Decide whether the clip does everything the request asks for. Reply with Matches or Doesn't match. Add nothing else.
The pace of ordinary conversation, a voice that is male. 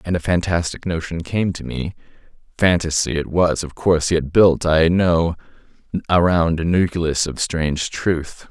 Matches